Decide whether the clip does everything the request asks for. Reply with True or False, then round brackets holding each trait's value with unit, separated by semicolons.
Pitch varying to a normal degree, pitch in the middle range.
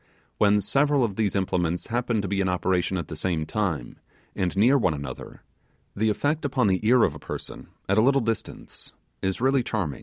False (5.0 semitones; 100 Hz)